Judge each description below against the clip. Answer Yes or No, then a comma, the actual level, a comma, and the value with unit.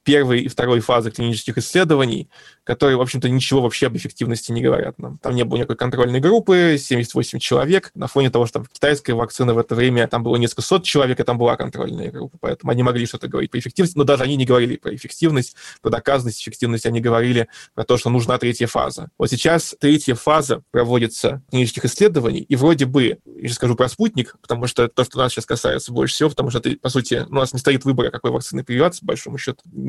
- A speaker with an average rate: No, fast, 215 wpm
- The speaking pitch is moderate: No, low, 125 Hz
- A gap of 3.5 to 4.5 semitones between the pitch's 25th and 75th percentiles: No, average, 2.9 semitones